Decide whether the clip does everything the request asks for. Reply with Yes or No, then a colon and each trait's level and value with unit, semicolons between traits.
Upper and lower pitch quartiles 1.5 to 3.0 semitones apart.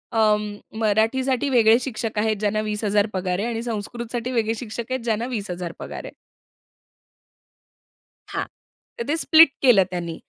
Yes: narrow, 2.4 semitones